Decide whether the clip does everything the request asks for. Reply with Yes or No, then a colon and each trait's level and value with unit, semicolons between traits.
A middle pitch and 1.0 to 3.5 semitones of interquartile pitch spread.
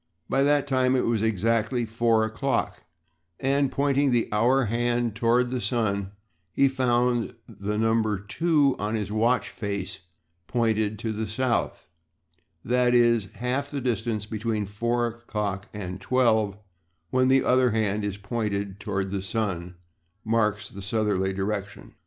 No: low, 115 Hz; average, 3.1 semitones